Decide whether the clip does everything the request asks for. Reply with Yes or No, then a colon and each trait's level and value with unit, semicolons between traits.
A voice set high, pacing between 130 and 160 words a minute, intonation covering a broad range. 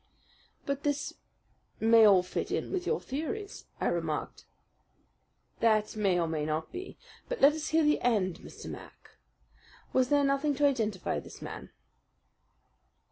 Yes: very high, 265 Hz; average, 145 wpm; wide, 6.3 semitones